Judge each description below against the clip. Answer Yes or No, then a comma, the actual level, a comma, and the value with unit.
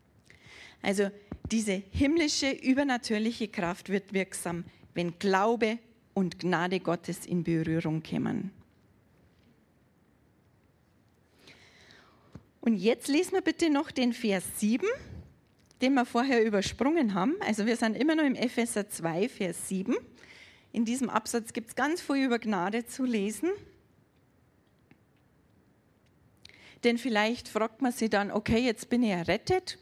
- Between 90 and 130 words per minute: Yes, slow, 125 wpm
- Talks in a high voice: Yes, high, 225 Hz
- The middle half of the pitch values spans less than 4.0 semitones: No, average, 4.3 semitones